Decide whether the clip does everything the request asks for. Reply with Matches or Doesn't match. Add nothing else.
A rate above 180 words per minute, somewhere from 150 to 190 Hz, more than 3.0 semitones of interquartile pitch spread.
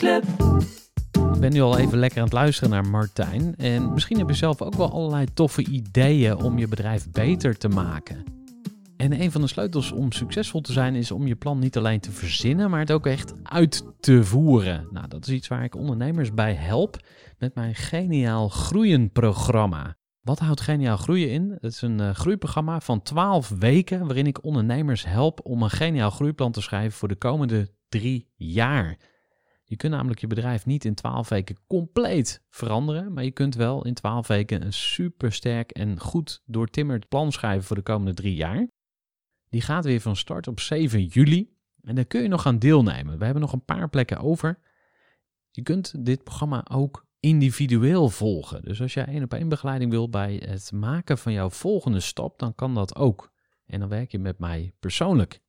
Doesn't match